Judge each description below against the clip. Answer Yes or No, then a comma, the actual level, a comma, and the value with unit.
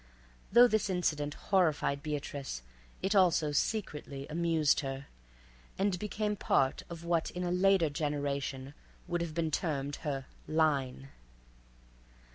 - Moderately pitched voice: Yes, medium, 155 Hz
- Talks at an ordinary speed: No, slow, 120 wpm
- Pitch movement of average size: Yes, average, 4.1 semitones